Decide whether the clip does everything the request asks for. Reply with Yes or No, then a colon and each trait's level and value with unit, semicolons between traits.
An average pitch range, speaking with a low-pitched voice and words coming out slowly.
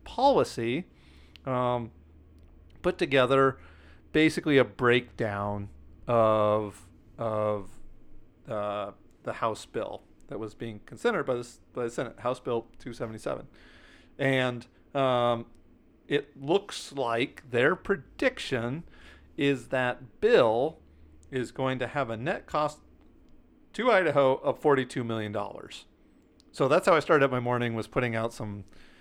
Yes: average, 4.3 semitones; low, 115 Hz; slow, 125 wpm